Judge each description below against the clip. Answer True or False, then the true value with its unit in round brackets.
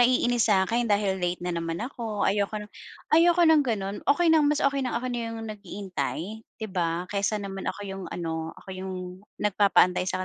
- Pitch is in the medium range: False (200 Hz)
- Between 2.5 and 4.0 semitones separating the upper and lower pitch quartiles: False (4.5 semitones)